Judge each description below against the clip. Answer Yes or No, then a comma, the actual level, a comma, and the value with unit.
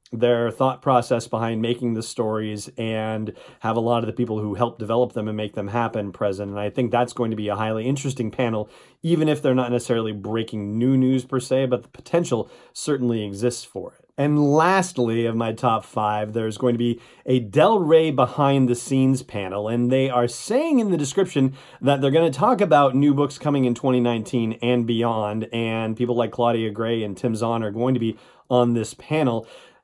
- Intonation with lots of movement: No, average, 2.9 semitones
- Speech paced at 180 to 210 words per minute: Yes, fast, 205 wpm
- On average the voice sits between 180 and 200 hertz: No, low, 120 Hz